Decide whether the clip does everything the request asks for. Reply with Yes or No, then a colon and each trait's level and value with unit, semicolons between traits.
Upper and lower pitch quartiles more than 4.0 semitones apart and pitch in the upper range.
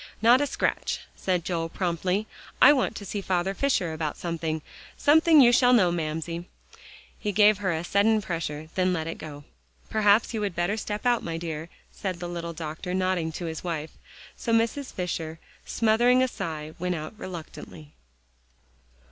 No: average, 4.7 semitones; medium, 180 Hz